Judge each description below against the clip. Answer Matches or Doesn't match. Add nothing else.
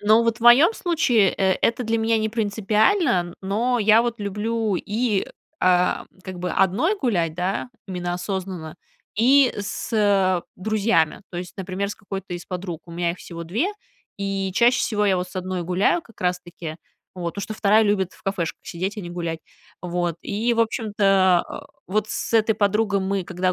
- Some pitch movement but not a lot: Matches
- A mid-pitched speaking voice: Doesn't match